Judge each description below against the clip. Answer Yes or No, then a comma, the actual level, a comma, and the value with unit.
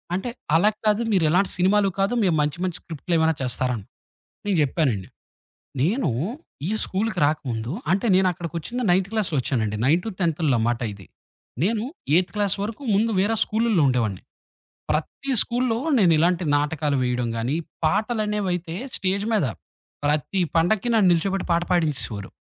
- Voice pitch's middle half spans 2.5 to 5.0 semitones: No, wide, 5.6 semitones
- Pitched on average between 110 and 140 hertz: No, medium, 175 Hz